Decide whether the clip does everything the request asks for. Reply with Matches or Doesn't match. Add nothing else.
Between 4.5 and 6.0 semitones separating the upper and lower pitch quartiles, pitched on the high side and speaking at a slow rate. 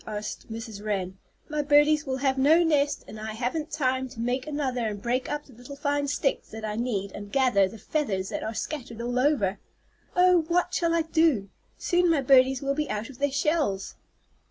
Doesn't match